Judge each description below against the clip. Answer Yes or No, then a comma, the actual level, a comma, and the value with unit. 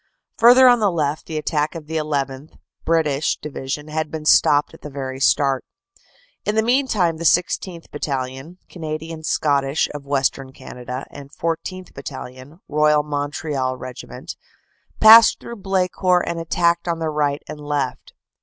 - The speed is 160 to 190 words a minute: No, average, 145 wpm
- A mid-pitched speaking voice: Yes, medium, 150 Hz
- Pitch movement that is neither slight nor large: Yes, average, 3.3 semitones